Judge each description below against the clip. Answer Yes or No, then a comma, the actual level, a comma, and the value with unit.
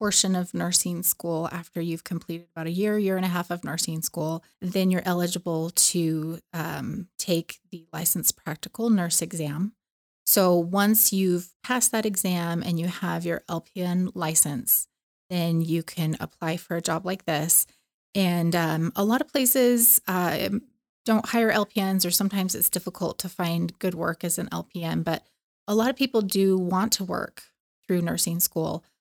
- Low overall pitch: No, medium, 180 Hz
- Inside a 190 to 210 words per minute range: No, average, 170 wpm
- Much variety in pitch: No, average, 2.9 semitones